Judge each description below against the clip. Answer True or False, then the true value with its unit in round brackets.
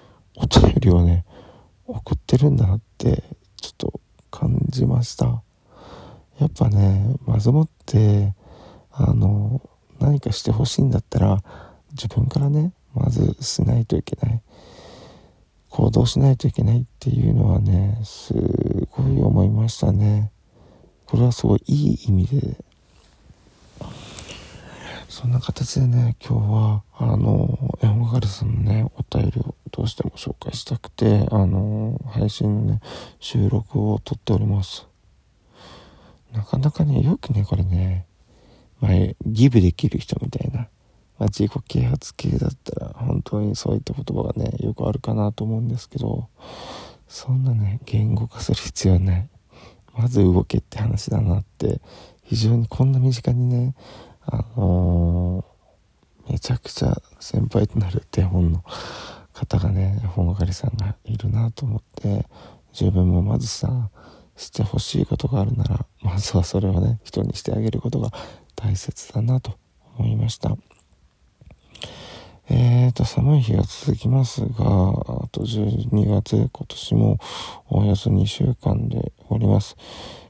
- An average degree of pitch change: True (3.9 semitones)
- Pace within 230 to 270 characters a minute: True (260 characters per minute)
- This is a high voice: False (110 Hz)